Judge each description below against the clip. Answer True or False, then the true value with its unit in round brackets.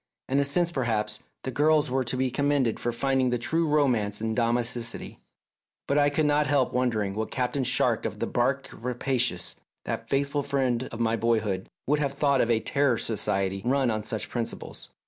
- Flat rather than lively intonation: False (3.7 semitones)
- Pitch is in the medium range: False (125 Hz)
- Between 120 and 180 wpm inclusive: False (195 wpm)